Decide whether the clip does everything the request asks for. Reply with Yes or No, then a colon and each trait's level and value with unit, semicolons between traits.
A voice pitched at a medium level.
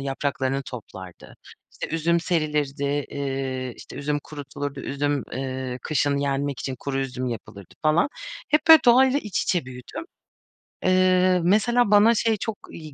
Yes: medium, 145 Hz